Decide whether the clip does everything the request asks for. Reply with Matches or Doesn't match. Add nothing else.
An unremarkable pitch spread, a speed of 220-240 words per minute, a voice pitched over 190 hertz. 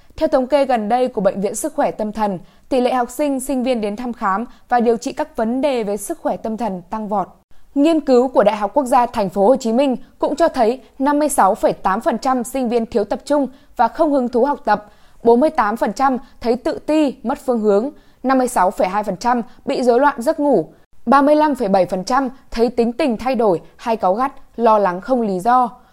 Doesn't match